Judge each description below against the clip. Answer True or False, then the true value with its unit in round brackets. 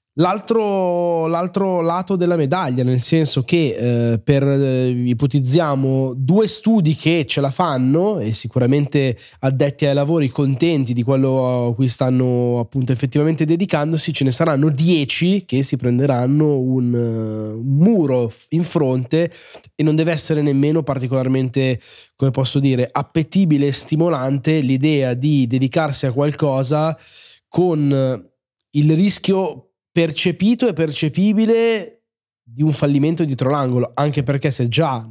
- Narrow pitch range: False (4.0 semitones)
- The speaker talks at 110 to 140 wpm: True (130 wpm)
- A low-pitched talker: False (145 Hz)